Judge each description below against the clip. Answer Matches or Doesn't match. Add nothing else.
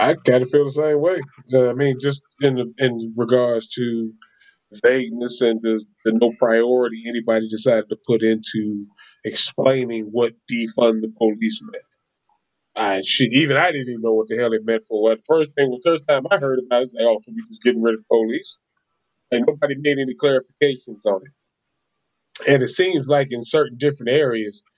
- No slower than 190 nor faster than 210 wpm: Matches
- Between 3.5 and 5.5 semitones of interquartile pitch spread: Matches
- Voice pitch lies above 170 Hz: Doesn't match